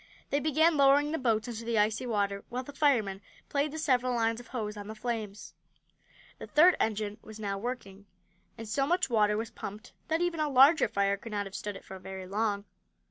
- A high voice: Yes, high, 225 Hz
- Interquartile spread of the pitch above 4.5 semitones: Yes, average, 5.1 semitones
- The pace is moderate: No, fast, 210 wpm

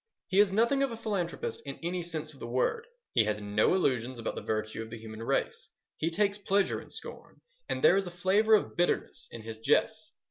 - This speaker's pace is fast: Yes, fast, 220 wpm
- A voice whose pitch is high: No, medium, 175 Hz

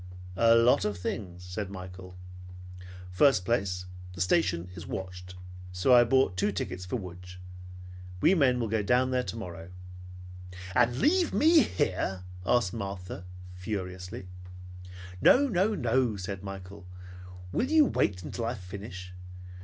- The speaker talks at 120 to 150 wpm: Yes, slow, 135 wpm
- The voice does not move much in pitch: No, average, 5.0 semitones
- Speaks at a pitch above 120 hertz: No, low, 100 Hz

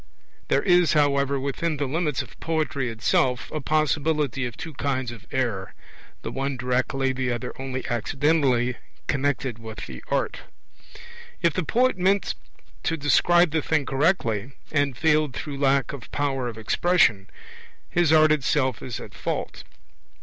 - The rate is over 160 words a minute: No, average, 150 wpm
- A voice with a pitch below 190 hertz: Yes, medium, 140 Hz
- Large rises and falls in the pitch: No, average, 3.6 semitones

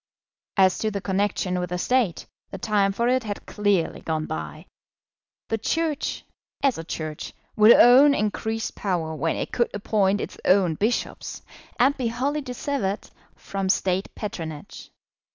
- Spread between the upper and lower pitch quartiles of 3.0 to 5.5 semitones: Yes, average, 4.6 semitones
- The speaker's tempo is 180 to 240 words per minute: No, average, 150 wpm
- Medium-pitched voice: No, high, 205 Hz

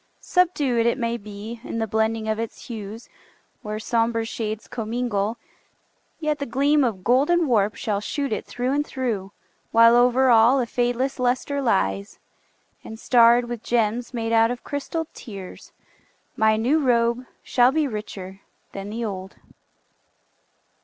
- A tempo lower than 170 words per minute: Yes, average, 145 wpm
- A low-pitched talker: No, high, 235 Hz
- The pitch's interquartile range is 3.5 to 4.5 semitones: No, average, 2.7 semitones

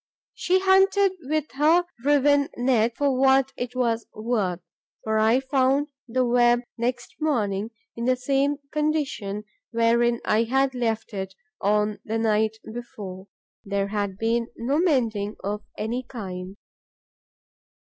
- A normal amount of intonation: Yes, average, 4.0 semitones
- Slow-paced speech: Yes, slow, 130 wpm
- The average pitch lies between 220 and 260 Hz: Yes, high, 240 Hz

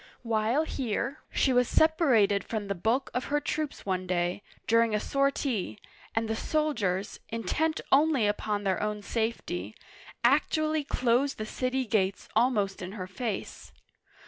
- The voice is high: Yes, high, 230 Hz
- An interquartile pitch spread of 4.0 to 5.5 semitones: Yes, average, 5.2 semitones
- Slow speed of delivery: No, average, 145 wpm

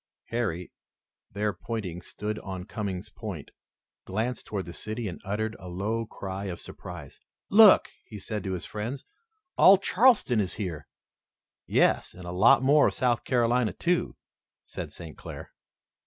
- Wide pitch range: No, average, 4.3 semitones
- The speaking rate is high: No, average, 150 wpm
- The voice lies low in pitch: Yes, low, 105 Hz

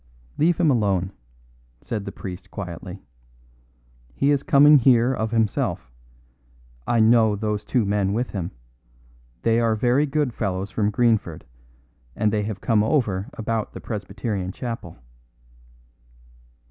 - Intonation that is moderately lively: Yes, average, 3.4 semitones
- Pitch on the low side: Yes, low, 110 Hz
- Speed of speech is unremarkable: No, slow, 130 wpm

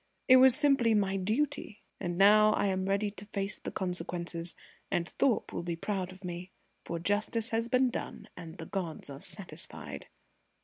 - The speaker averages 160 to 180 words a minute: Yes, average, 175 wpm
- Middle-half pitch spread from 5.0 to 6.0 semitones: No, average, 4.0 semitones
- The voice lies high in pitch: Yes, high, 195 Hz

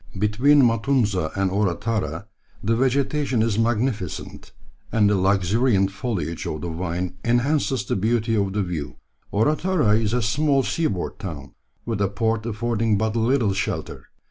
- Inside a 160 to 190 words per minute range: No, average, 145 wpm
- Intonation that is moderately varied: Yes, average, 3.7 semitones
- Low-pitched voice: Yes, low, 110 Hz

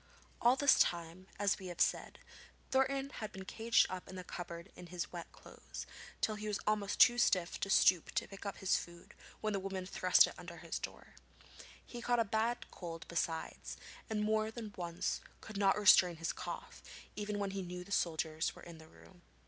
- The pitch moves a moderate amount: Yes, average, 3.6 semitones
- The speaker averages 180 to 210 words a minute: Yes, average, 200 wpm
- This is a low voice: No, high, 195 Hz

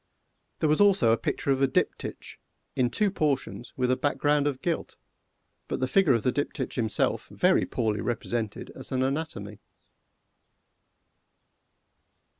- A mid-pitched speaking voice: No, low, 130 Hz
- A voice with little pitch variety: No, average, 3.7 semitones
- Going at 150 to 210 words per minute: No, average, 140 wpm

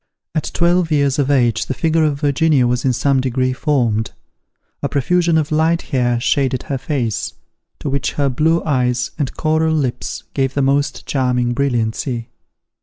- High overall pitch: No, medium, 140 Hz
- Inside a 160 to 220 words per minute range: Yes, average, 165 wpm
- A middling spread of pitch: Yes, average, 3.6 semitones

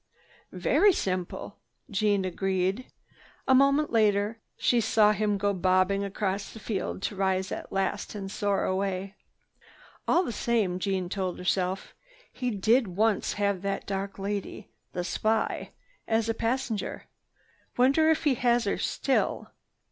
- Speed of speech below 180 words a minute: Yes, average, 140 wpm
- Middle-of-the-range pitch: No, high, 200 Hz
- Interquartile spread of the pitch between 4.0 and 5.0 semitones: No, average, 2.9 semitones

